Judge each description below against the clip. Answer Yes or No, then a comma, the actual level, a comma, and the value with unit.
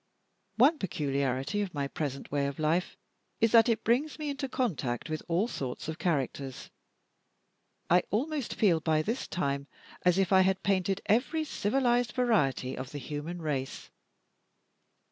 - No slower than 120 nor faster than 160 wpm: Yes, average, 150 wpm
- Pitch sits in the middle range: Yes, medium, 180 Hz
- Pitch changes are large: Yes, wide, 8.3 semitones